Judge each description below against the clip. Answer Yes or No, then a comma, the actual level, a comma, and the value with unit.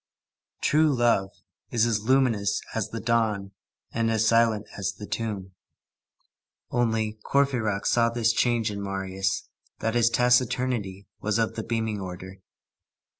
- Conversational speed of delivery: No, slow, 130 wpm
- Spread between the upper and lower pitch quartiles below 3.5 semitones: Yes, average, 2.7 semitones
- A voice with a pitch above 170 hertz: No, low, 110 Hz